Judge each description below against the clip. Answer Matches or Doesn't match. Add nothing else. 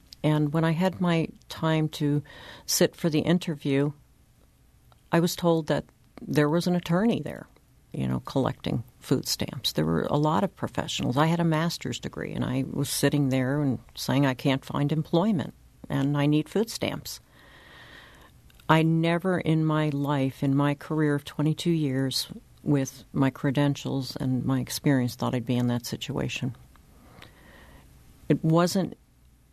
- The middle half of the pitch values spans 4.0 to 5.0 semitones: Doesn't match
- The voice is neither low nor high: Matches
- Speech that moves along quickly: Doesn't match